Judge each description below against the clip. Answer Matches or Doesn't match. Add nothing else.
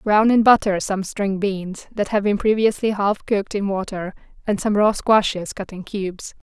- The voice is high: Matches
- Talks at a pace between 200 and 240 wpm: Doesn't match